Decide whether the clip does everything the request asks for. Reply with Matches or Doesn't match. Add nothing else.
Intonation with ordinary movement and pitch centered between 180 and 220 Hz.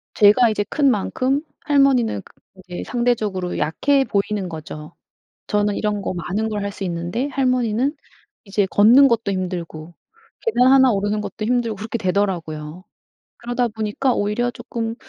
Matches